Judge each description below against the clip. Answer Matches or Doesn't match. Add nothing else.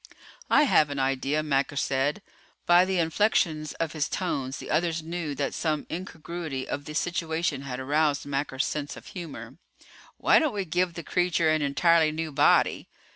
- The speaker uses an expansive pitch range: Doesn't match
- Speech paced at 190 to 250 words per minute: Doesn't match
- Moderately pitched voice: Matches